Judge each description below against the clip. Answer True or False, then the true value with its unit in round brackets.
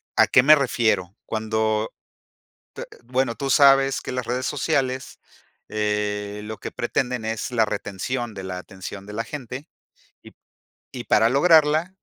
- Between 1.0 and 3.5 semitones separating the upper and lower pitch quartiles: False (4.4 semitones)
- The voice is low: True (120 Hz)